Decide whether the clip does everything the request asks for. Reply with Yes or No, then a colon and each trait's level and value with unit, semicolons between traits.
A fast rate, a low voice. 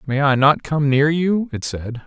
No: fast, 235 wpm; medium, 145 Hz